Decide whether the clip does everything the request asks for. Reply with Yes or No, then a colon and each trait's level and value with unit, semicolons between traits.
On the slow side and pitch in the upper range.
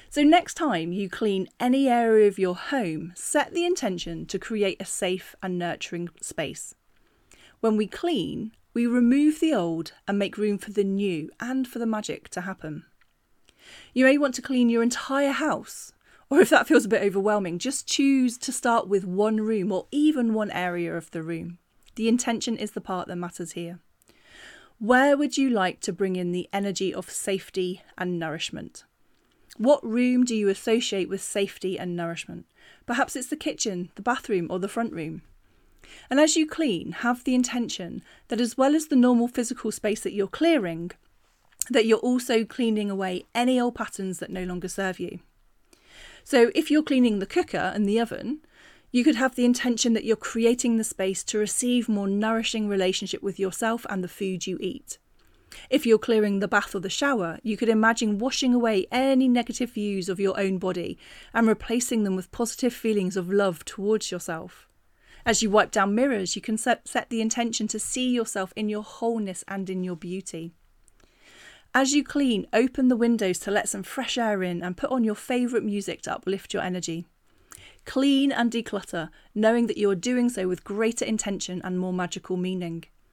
No: average, 185 wpm; high, 215 Hz